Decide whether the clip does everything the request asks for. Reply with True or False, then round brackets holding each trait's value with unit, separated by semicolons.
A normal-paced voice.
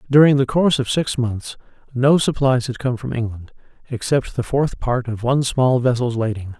True (190 wpm)